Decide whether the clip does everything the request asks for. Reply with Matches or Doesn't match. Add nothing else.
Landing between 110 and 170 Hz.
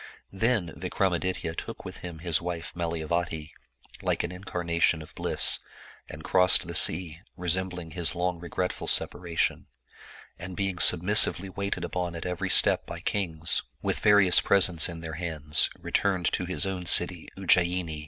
Doesn't match